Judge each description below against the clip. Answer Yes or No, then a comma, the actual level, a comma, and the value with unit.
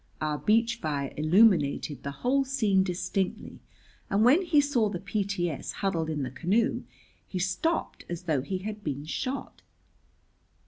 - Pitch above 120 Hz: Yes, high, 190 Hz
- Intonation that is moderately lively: No, wide, 6.3 semitones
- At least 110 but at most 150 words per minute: Yes, average, 145 wpm